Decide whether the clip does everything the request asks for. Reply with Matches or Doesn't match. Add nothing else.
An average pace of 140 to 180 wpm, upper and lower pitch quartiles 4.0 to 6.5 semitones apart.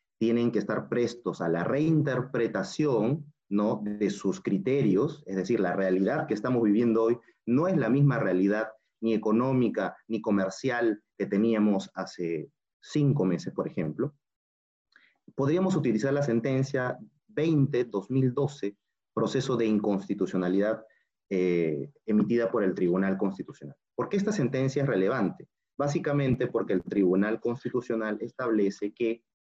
Doesn't match